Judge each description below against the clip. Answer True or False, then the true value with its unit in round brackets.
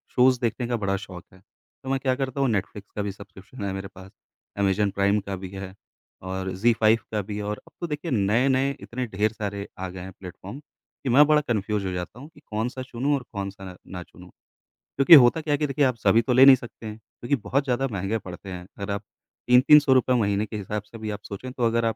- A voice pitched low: True (110 Hz)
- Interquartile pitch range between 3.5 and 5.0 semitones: True (4.6 semitones)